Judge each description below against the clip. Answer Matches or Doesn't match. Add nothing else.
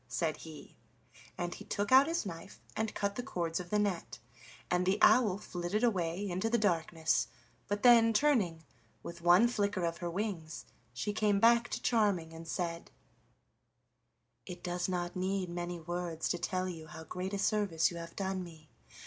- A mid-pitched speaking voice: Matches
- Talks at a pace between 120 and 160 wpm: Doesn't match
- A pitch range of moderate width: Matches